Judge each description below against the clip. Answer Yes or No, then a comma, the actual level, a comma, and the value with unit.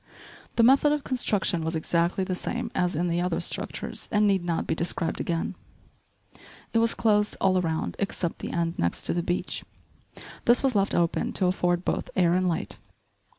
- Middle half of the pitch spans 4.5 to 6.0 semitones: No, average, 3.5 semitones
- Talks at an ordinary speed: Yes, average, 185 wpm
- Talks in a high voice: No, medium, 180 Hz